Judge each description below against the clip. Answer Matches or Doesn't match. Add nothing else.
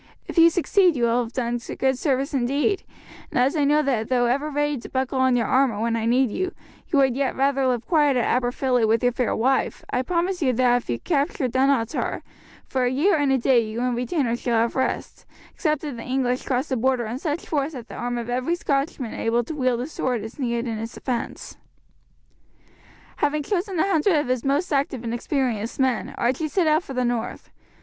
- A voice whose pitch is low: Doesn't match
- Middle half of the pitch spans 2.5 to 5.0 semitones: Matches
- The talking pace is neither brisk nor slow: Doesn't match